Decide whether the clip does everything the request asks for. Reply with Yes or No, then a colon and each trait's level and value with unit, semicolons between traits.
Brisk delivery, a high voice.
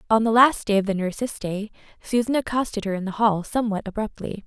Yes: fast, 215 wpm; high, 215 Hz